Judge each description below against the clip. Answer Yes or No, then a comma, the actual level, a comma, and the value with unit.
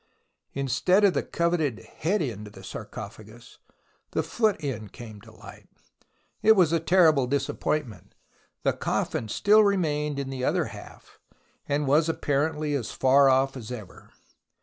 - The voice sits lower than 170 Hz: Yes, medium, 140 Hz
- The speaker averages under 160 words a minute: Yes, average, 150 wpm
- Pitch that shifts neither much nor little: Yes, average, 5.0 semitones